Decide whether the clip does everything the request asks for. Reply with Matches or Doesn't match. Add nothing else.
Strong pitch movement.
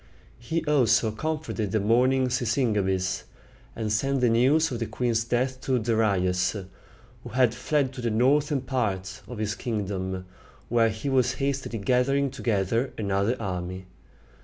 Doesn't match